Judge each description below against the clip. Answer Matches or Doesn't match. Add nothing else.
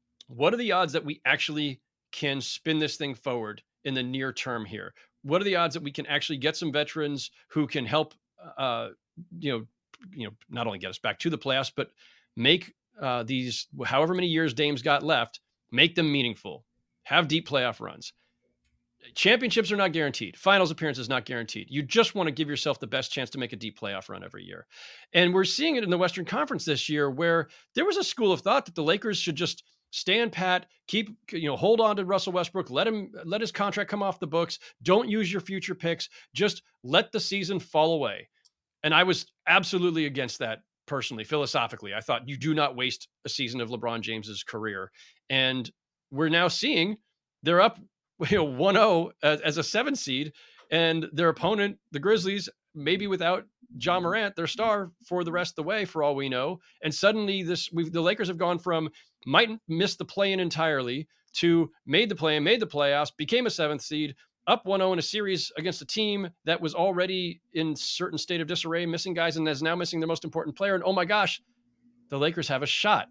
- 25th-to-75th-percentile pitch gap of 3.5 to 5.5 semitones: Matches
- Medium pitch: Matches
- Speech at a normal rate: Doesn't match